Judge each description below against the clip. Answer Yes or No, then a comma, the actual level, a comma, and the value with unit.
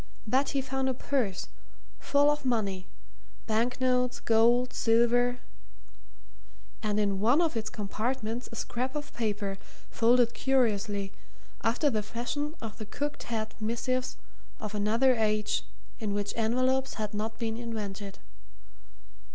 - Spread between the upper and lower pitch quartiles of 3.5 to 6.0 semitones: No, average, 3.1 semitones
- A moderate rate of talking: No, slow, 125 wpm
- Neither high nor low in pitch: No, high, 230 Hz